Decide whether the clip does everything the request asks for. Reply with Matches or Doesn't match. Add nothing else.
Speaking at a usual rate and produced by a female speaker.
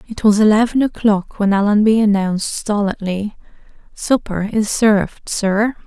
Doesn't match